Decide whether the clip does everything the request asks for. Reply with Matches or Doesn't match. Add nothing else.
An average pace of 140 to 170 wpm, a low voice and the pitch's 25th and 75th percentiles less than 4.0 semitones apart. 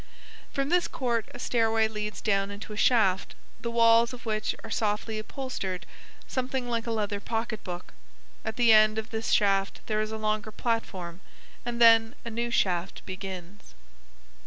Doesn't match